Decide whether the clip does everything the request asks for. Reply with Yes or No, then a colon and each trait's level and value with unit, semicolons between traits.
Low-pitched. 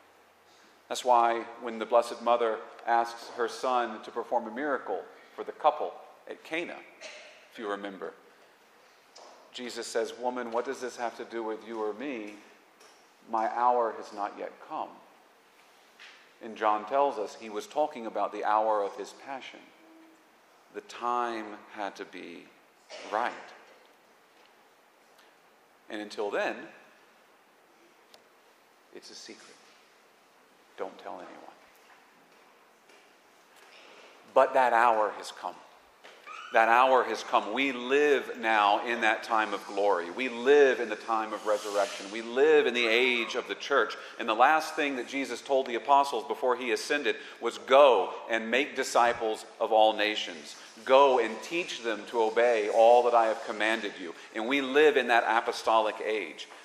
Yes: low, 115 Hz